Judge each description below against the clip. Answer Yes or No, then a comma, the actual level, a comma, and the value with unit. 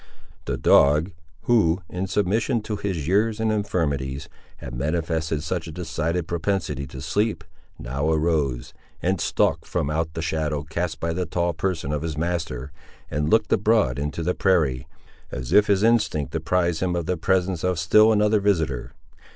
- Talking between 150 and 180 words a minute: Yes, average, 165 wpm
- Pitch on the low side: Yes, very low, 85 Hz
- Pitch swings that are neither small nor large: Yes, average, 3.9 semitones